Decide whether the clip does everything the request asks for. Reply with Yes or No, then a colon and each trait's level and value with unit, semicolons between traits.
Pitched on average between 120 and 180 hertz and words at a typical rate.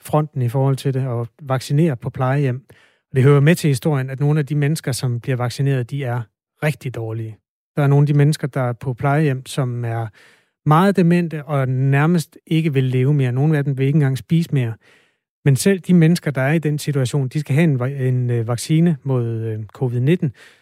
Yes: medium, 140 Hz; average, 205 wpm